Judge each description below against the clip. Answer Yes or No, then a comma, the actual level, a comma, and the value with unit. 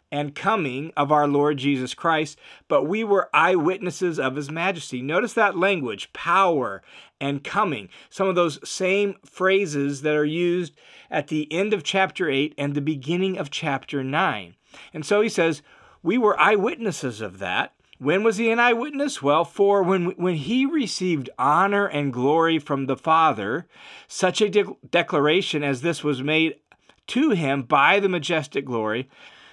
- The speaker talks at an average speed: Yes, average, 165 wpm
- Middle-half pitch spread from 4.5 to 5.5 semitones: Yes, average, 5.1 semitones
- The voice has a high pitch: No, medium, 165 Hz